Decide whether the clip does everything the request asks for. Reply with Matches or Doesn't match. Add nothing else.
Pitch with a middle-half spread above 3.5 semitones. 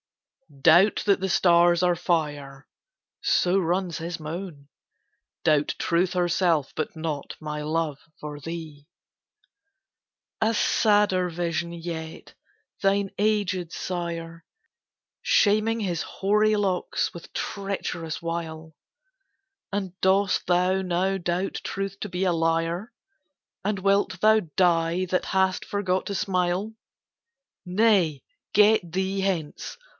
Doesn't match